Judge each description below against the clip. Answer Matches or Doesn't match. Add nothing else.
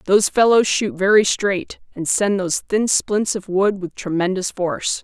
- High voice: Matches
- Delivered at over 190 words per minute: Doesn't match